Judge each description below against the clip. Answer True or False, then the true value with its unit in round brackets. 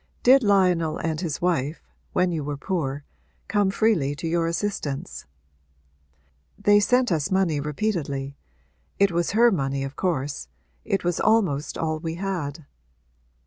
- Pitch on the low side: False (170 Hz)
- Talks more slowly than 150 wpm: True (140 wpm)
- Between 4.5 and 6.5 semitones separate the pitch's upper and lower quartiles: True (5.1 semitones)